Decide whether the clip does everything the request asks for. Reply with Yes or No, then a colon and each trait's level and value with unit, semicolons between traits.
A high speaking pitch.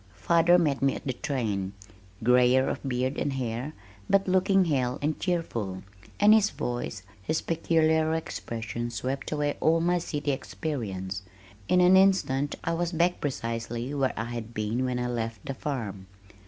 No: low, 135 Hz